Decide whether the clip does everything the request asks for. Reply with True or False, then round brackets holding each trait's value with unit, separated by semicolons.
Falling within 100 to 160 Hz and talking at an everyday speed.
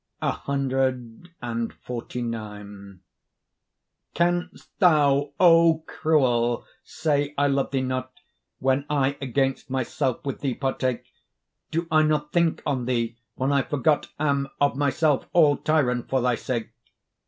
False (135 Hz; 120 wpm)